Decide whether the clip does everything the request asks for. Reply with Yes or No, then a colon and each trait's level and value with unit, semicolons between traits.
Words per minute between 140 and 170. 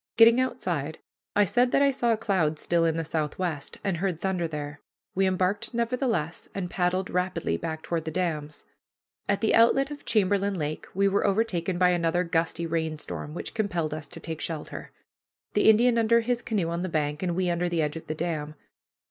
No: average, 190 wpm